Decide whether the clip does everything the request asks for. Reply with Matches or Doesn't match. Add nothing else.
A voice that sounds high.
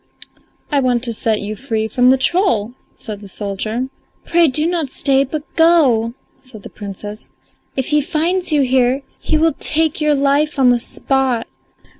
Matches